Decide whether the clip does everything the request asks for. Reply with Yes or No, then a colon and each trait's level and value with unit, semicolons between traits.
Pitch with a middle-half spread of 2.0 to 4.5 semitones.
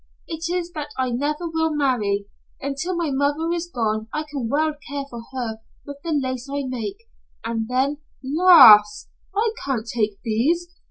No: average, 5.2 semitones